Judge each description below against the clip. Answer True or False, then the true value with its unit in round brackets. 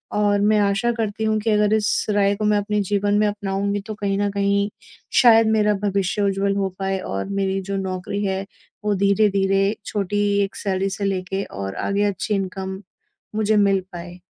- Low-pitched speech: False (200 Hz)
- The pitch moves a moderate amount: False (1.2 semitones)